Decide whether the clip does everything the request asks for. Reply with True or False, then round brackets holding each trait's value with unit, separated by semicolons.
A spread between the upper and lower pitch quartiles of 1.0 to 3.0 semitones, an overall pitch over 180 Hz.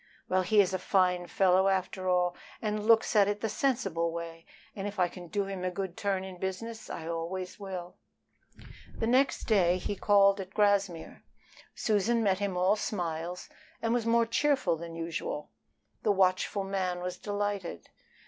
True (2.5 semitones; 190 Hz)